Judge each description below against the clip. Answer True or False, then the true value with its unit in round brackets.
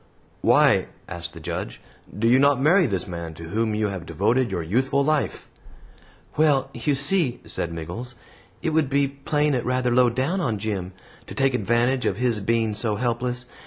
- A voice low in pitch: True (125 Hz)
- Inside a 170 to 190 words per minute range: True (180 wpm)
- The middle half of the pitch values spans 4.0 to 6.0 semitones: True (4.5 semitones)